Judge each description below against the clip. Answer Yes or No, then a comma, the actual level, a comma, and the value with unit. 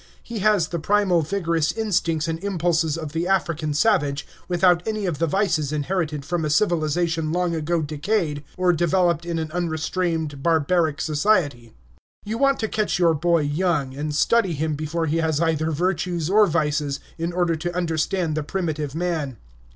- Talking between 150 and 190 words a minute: Yes, average, 165 wpm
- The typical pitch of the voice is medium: Yes, medium, 165 Hz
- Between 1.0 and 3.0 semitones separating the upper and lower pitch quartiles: Yes, average, 2.7 semitones